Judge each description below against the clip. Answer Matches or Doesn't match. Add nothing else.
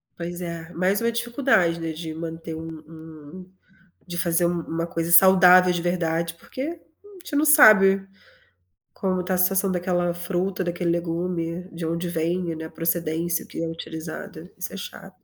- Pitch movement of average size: Doesn't match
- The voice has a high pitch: Doesn't match